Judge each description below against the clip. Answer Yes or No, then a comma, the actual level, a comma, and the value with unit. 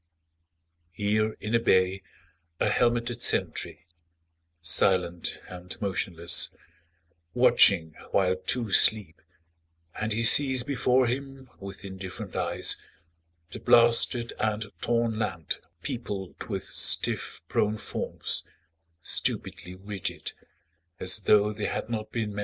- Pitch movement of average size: Yes, average, 3.9 semitones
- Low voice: Yes, low, 105 Hz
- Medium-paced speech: No, slow, 110 wpm